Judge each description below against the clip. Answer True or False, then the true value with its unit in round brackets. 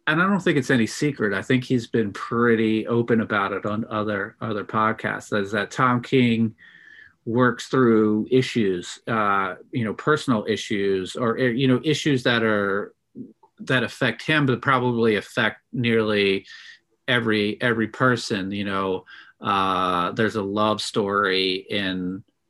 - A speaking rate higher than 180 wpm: False (150 wpm)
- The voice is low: True (115 Hz)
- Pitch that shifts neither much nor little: True (3.5 semitones)